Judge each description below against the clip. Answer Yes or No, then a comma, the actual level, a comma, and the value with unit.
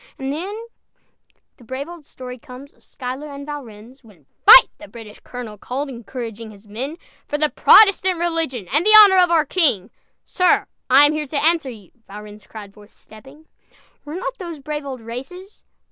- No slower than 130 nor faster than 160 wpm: No, average, 175 wpm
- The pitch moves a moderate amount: No, wide, 6.2 semitones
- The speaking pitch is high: Yes, very high, 275 Hz